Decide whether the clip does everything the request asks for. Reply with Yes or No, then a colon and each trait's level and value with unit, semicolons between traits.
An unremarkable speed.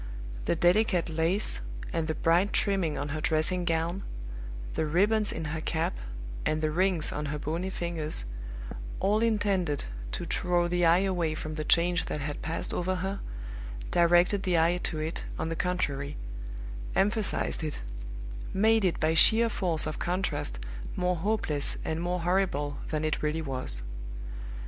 Yes: average, 155 wpm